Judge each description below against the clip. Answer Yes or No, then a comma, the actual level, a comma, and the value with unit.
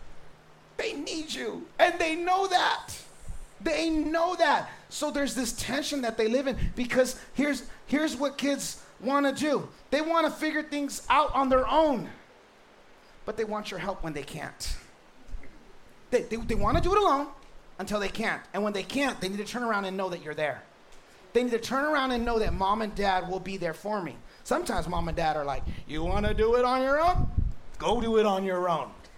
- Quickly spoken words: Yes, fast, 215 wpm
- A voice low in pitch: No, high, 245 Hz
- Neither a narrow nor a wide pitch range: No, wide, 6.7 semitones